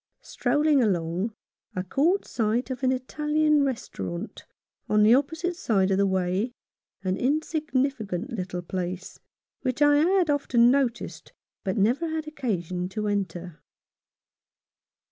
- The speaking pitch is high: Yes, high, 235 Hz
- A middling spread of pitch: No, wide, 7.5 semitones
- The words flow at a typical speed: No, slow, 125 wpm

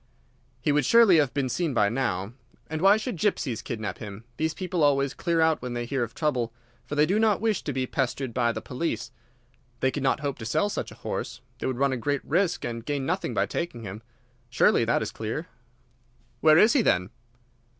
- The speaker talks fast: Yes, fast, 215 wpm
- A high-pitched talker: No, medium, 140 Hz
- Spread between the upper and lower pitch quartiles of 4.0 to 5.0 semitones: No, wide, 5.5 semitones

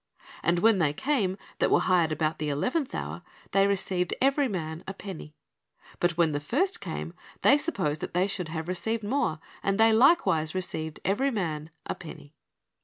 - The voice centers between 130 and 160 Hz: No, medium, 185 Hz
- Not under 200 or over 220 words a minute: No, average, 180 wpm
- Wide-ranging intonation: Yes, wide, 5.8 semitones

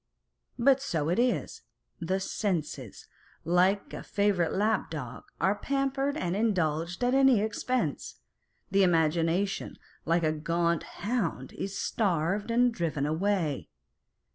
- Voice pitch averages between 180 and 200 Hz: Yes, high, 190 Hz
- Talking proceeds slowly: Yes, slow, 120 wpm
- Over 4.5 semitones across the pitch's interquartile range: Yes, average, 5.0 semitones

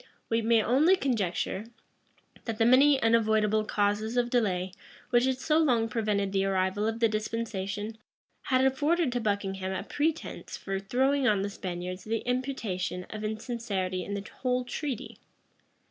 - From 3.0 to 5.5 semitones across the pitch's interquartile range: Yes, average, 4.0 semitones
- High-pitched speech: Yes, high, 220 Hz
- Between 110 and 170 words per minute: Yes, average, 150 wpm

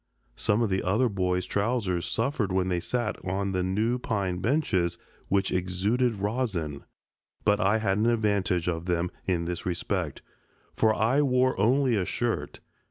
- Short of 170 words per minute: Yes, average, 160 wpm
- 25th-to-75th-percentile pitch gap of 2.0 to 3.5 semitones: No, average, 3.9 semitones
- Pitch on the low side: Yes, low, 100 Hz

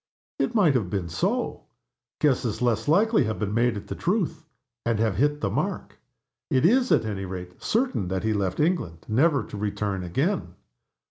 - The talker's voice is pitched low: Yes, low, 115 Hz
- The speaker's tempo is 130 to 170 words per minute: No, average, 180 wpm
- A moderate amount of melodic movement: No, wide, 8.0 semitones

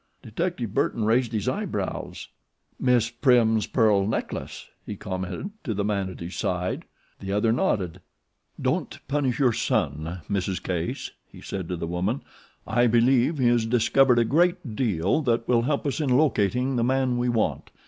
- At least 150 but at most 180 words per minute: Yes, average, 165 wpm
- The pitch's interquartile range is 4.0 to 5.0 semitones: Yes, average, 4.5 semitones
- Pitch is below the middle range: Yes, low, 115 Hz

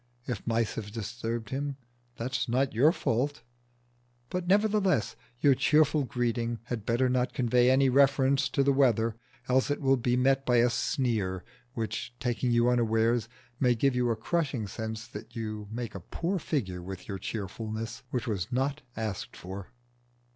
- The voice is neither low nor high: No, low, 120 Hz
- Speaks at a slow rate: No, average, 165 wpm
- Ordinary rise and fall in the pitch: Yes, average, 3.2 semitones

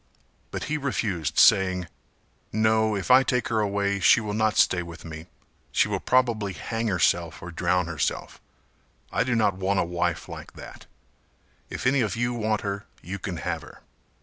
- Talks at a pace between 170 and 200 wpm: Yes, average, 175 wpm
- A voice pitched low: Yes, low, 100 Hz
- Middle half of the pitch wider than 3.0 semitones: Yes, average, 4.2 semitones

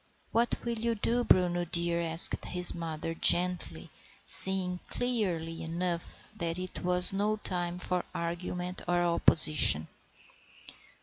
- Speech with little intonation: Yes, narrow, 1.6 semitones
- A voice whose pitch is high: No, medium, 180 Hz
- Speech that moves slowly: Yes, slow, 120 wpm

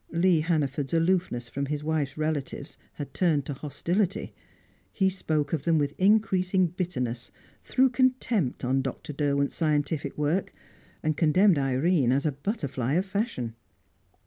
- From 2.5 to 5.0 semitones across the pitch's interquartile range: Yes, average, 4.6 semitones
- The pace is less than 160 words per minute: Yes, average, 140 wpm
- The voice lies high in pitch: No, medium, 155 Hz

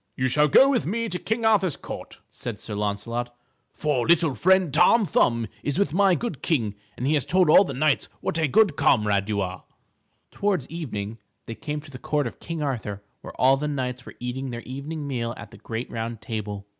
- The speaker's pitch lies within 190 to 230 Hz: No, low, 135 Hz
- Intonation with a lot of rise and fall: Yes, wide, 6.2 semitones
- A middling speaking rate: No, fast, 210 wpm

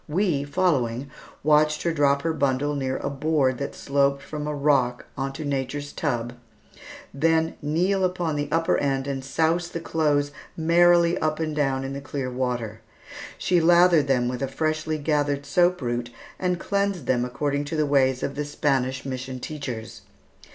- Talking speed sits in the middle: Yes, average, 165 wpm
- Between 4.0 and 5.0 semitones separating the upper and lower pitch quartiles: No, average, 3.1 semitones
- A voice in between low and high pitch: Yes, medium, 145 Hz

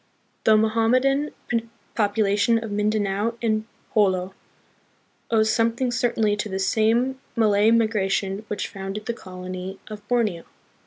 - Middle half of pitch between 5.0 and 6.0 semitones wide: No, narrow, 2.5 semitones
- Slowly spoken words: Yes, slow, 120 wpm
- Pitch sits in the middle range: No, high, 215 Hz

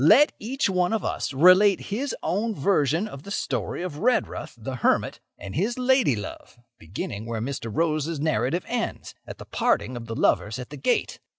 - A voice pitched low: No, medium, 160 Hz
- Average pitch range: No, wide, 8.6 semitones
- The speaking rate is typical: Yes, average, 180 wpm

